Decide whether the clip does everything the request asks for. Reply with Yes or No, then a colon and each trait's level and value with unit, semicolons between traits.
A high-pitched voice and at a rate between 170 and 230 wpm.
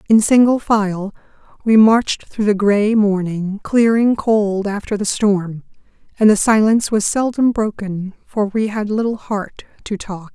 No: high, 210 Hz; average, 155 wpm